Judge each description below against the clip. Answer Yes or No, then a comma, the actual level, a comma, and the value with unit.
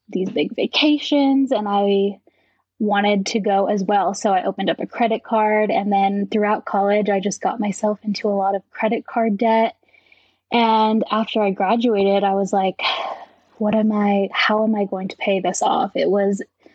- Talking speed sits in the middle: Yes, average, 185 wpm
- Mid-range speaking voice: No, high, 210 Hz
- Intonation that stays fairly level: Yes, narrow, 1.9 semitones